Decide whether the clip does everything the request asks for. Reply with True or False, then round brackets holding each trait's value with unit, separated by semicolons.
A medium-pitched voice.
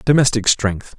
False (115 Hz)